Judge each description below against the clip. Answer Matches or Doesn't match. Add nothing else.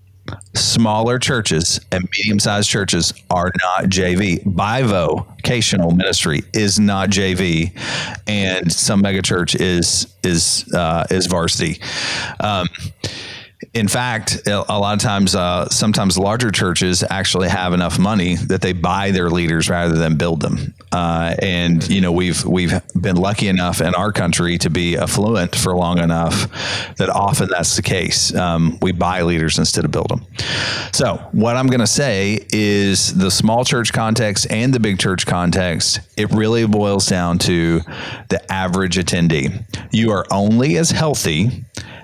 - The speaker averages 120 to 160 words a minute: Matches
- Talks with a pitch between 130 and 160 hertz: Doesn't match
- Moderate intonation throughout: Matches